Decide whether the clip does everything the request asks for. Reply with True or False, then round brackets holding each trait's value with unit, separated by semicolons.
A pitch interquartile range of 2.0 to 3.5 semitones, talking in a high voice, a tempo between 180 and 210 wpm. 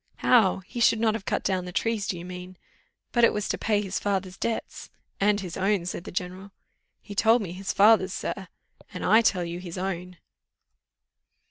True (2.5 semitones; 195 Hz; 205 wpm)